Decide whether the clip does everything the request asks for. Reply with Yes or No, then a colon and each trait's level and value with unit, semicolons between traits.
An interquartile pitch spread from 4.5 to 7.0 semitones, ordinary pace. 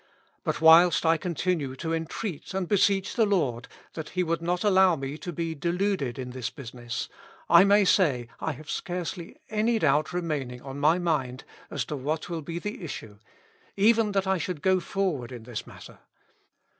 Yes: average, 5.2 semitones; average, 180 wpm